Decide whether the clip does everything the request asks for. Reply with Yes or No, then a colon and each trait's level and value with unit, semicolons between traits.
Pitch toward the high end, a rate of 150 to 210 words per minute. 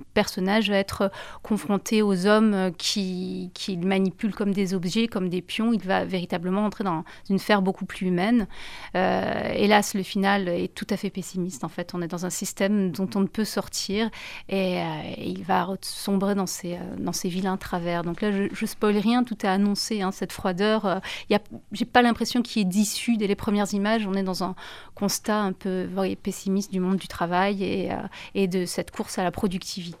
Yes: high, 195 Hz; fast, 205 wpm